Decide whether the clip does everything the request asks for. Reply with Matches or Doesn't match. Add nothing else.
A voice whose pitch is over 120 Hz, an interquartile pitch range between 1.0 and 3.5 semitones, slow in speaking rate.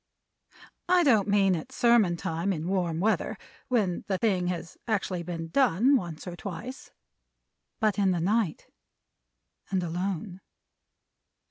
Doesn't match